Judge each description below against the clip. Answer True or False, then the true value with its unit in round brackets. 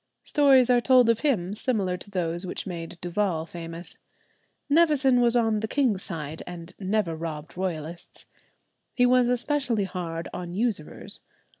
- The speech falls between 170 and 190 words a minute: False (145 wpm)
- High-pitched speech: True (195 Hz)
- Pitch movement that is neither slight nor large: False (6.3 semitones)